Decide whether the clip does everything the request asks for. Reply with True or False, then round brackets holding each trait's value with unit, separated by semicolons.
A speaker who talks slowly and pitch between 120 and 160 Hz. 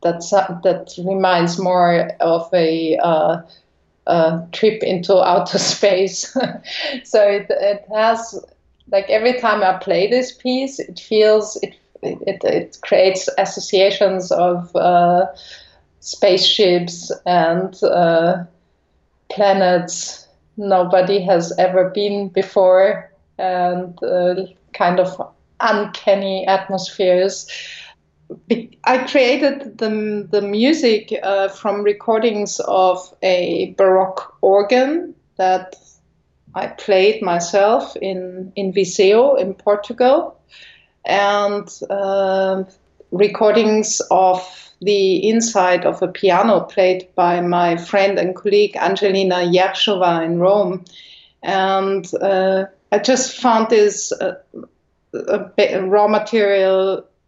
False (100 wpm; 190 Hz)